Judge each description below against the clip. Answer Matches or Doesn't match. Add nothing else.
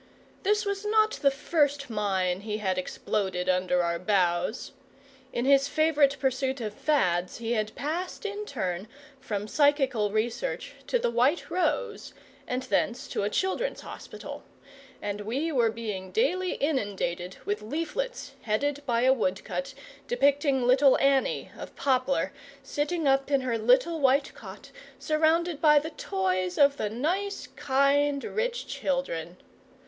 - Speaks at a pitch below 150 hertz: Doesn't match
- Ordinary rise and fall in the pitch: Doesn't match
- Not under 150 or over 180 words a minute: Doesn't match